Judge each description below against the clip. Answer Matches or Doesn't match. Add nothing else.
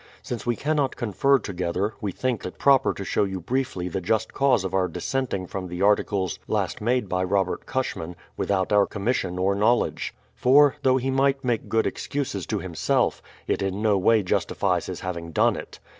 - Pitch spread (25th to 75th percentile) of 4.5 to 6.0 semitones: Matches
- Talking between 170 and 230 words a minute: Matches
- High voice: Doesn't match